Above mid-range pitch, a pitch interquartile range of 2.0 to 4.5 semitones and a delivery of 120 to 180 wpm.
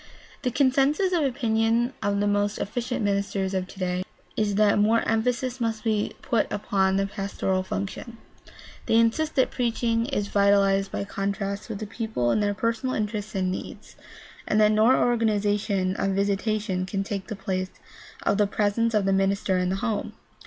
Yes: high, 205 Hz; narrow, 2.6 semitones; average, 175 wpm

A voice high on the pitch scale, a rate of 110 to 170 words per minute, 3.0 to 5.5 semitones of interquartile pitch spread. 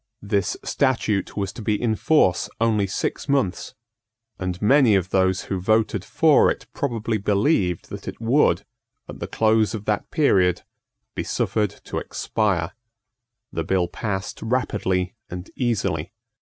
No: low, 105 Hz; average, 140 wpm; average, 3.3 semitones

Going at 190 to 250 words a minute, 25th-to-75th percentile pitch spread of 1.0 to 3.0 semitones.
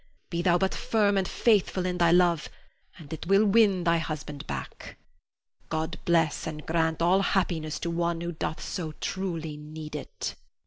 No: average, 170 wpm; narrow, 2.6 semitones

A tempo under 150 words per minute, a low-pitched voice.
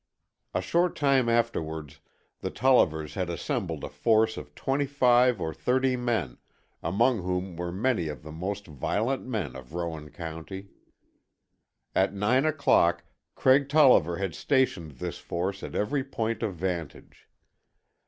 Yes: average, 140 wpm; low, 100 Hz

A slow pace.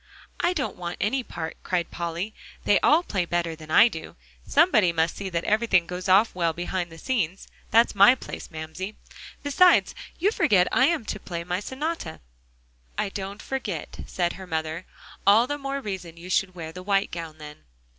No: average, 185 wpm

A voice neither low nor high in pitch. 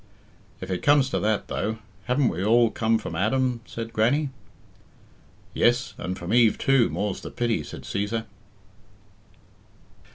No: low, 115 Hz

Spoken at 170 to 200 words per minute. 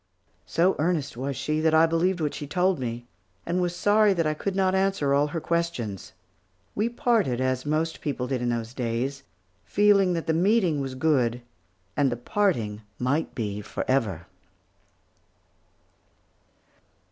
No: average, 150 wpm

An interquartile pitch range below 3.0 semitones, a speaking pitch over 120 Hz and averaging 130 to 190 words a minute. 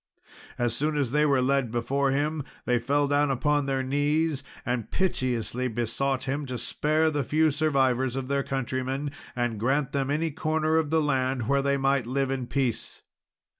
Yes: narrow, 2.4 semitones; low, 135 Hz; average, 175 wpm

